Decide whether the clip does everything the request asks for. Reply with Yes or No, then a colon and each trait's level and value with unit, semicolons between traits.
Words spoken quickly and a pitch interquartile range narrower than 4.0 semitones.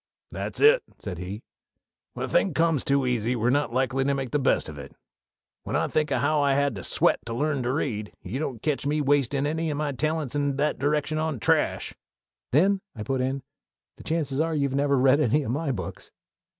Yes: fast, 215 wpm; average, 3.0 semitones